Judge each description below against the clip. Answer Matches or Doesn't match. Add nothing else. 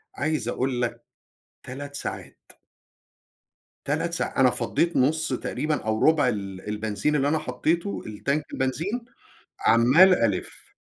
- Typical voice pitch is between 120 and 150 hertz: Matches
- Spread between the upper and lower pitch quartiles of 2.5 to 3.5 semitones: Doesn't match